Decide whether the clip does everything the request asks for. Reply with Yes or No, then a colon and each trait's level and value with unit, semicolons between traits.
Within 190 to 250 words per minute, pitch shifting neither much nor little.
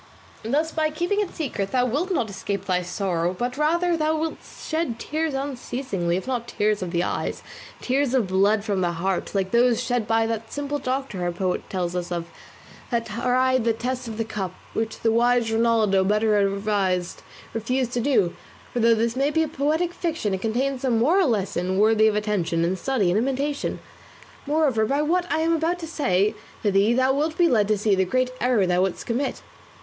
No: average, 200 wpm; wide, 5.7 semitones